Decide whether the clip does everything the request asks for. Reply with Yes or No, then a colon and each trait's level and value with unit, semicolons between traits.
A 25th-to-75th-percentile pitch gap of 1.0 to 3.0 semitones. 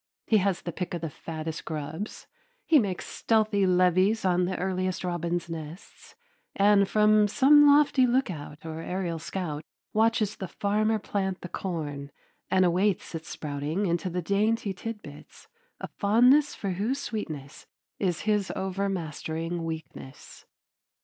No: average, 4.2 semitones